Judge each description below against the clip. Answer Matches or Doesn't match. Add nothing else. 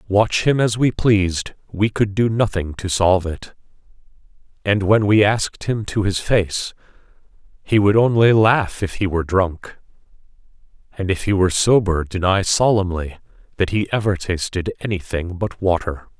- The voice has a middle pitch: Doesn't match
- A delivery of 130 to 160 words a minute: Matches